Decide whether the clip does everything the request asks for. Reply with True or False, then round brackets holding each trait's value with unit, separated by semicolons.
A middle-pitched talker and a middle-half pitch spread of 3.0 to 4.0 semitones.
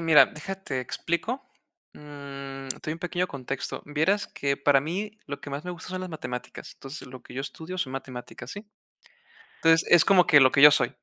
False (150 Hz; 4.4 semitones)